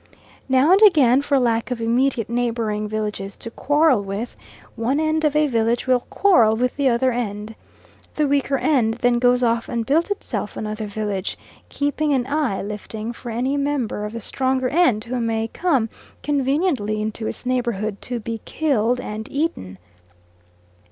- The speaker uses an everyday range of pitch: Yes, average, 4.1 semitones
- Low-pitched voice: No, high, 245 Hz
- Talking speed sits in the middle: Yes, average, 165 wpm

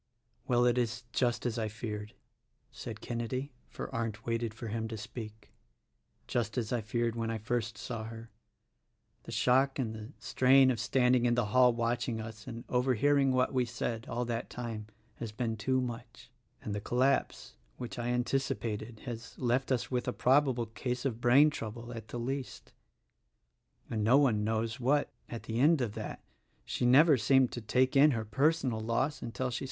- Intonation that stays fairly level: Yes, narrow, 2.2 semitones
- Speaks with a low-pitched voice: Yes, low, 120 Hz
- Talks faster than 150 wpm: Yes, average, 185 wpm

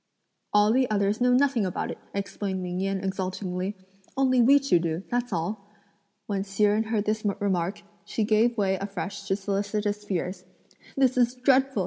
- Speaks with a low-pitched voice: No, high, 205 Hz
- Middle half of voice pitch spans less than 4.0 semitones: Yes, average, 3.5 semitones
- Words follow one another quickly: No, average, 165 wpm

